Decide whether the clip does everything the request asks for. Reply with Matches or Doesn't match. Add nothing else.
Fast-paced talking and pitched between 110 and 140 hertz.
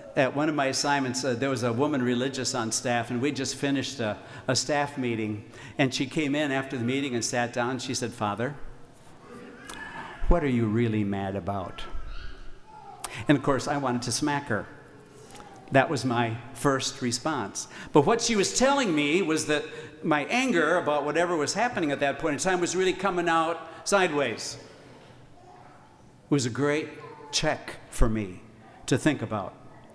Doesn't match